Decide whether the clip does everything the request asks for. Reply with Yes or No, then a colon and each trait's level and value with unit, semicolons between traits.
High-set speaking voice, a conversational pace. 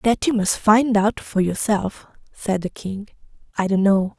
Yes: high, 205 Hz; average, 185 wpm